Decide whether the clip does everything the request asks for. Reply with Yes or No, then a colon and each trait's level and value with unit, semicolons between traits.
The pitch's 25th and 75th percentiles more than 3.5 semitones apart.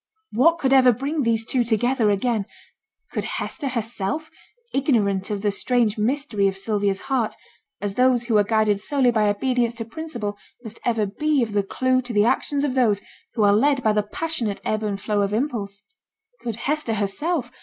Yes: average, 4.0 semitones